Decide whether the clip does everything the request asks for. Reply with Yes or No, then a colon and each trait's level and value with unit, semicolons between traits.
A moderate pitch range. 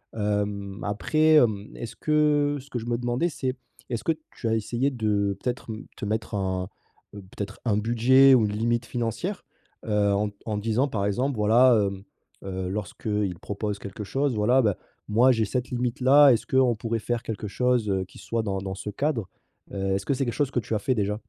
Yes: average, 3.6 semitones